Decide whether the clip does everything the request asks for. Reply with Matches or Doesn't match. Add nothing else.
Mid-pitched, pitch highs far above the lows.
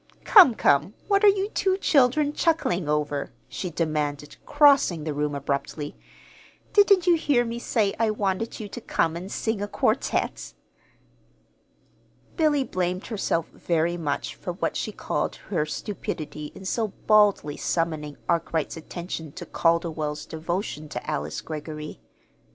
Matches